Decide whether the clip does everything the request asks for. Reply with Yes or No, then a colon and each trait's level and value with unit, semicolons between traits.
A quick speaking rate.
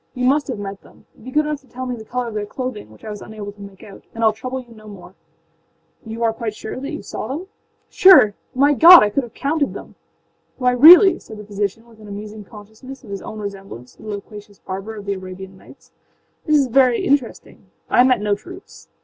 Yes: fast, 235 wpm